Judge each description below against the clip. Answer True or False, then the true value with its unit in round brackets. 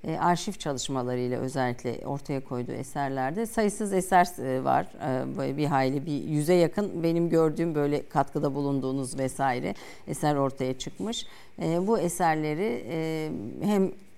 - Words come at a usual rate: True (115 wpm)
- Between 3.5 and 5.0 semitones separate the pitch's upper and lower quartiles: True (4.6 semitones)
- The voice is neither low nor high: True (150 Hz)